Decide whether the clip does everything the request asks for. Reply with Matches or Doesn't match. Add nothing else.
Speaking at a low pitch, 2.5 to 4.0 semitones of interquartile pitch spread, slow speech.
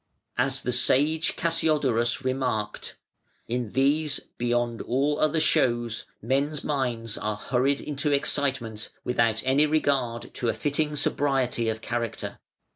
Matches